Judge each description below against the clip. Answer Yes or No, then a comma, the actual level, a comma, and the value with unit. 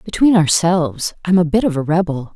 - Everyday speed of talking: No, fast, 230 wpm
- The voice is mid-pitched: Yes, medium, 170 Hz